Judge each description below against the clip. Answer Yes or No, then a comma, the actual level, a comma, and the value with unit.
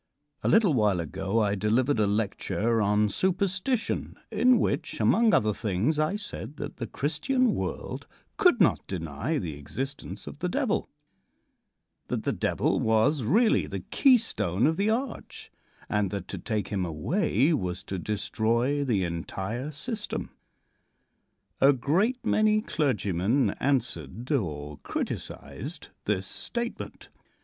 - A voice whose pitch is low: Yes, low, 120 Hz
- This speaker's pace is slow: Yes, slow, 130 wpm